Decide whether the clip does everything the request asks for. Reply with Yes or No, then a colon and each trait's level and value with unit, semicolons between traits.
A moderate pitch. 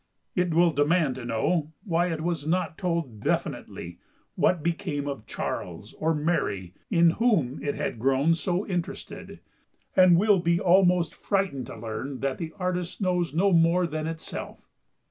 Yes: medium, 165 Hz